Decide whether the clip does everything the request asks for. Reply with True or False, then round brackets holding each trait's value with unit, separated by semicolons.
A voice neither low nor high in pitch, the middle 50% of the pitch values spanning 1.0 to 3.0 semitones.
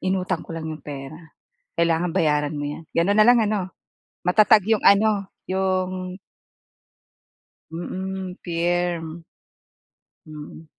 True (180 Hz; 2.7 semitones)